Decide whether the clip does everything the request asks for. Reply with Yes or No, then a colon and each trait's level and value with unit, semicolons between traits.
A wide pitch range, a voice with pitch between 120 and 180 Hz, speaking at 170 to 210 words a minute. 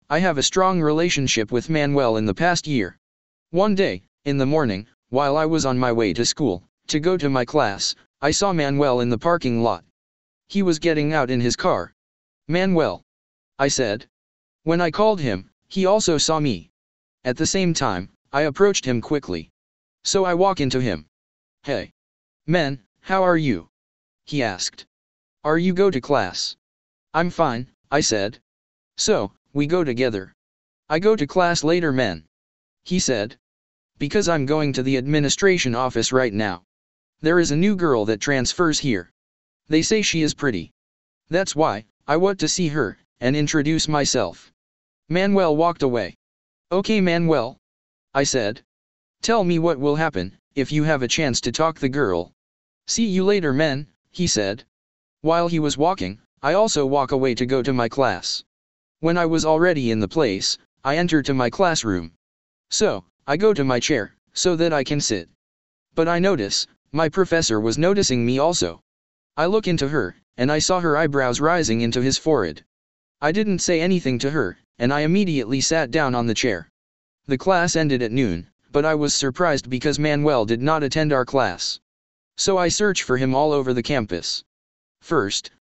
Yes: wide, 8.4 semitones; low, 135 Hz; average, 175 wpm